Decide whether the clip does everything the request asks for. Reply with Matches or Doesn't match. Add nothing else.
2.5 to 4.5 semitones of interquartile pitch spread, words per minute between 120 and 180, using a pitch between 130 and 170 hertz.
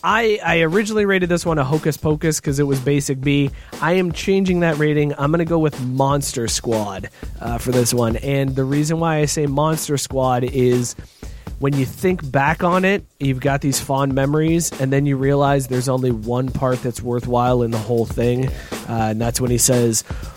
Doesn't match